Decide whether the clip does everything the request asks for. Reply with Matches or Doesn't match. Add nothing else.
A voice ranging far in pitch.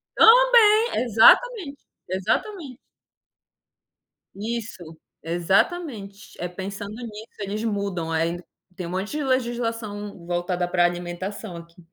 Matches